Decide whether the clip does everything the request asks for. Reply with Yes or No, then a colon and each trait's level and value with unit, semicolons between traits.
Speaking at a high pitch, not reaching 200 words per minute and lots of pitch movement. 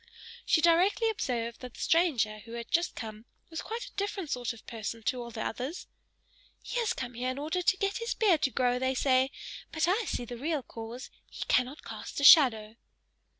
No: very high, 260 Hz; fast, 205 wpm; wide, 6.7 semitones